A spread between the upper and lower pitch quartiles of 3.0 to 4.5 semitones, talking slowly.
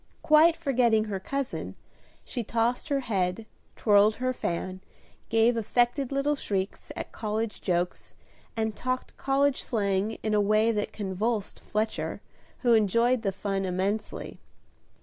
Yes: average, 3.7 semitones; slow, 130 wpm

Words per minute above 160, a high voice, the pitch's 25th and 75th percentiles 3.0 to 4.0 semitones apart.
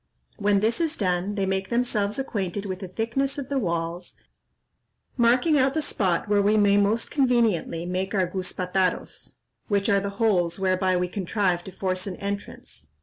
Yes: average, 170 wpm; high, 200 Hz; average, 3.5 semitones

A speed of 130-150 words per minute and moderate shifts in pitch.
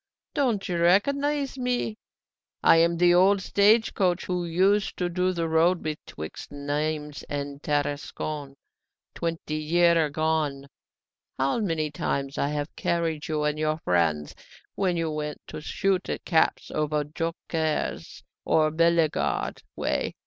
Yes: slow, 135 wpm; average, 3.2 semitones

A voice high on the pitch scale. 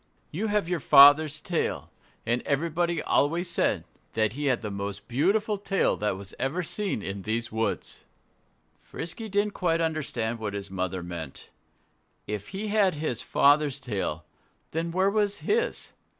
No: medium, 145 Hz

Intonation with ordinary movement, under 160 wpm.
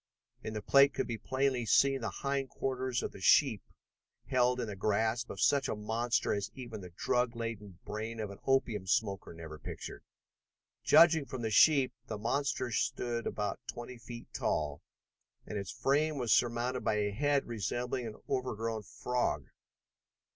No: average, 3.5 semitones; average, 165 wpm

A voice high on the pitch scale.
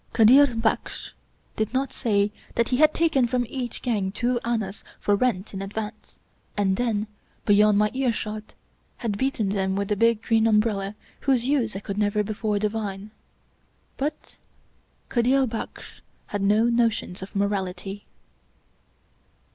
Yes: high, 215 Hz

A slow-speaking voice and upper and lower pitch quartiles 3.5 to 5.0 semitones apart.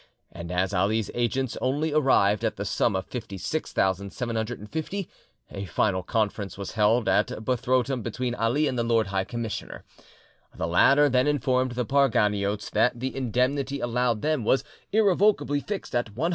No: average, 150 wpm; average, 4.5 semitones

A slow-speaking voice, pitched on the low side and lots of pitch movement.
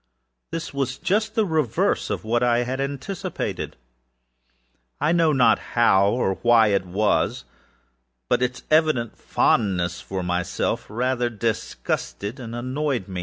Yes: slow, 120 wpm; low, 120 Hz; wide, 5.7 semitones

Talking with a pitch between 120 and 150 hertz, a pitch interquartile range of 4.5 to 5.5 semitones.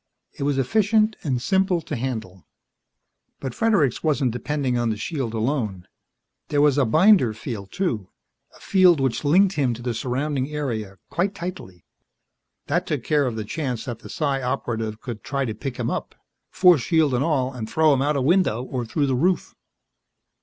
Yes: low, 135 Hz; average, 4.8 semitones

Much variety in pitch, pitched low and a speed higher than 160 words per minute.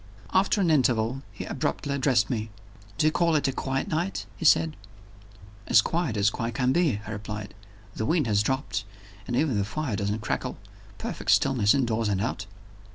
Yes: wide, 6.1 semitones; low, 125 Hz; average, 180 wpm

